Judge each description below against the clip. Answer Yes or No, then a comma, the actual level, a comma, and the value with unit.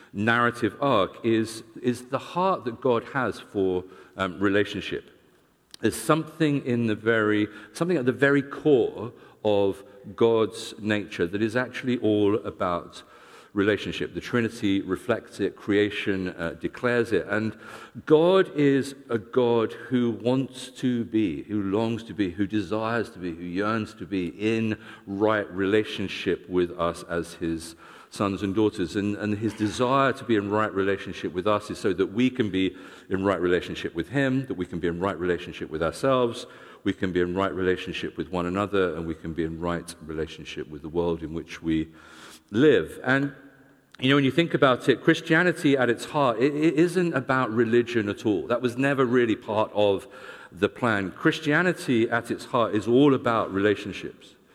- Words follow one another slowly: No, average, 175 wpm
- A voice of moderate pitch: No, low, 110 Hz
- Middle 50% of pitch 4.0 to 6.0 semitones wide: Yes, average, 4.6 semitones